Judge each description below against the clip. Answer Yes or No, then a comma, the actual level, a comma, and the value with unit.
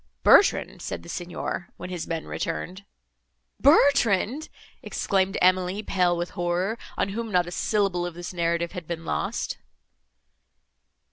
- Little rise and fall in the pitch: Yes, narrow, 2.3 semitones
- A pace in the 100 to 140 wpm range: Yes, slow, 135 wpm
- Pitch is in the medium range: Yes, medium, 180 Hz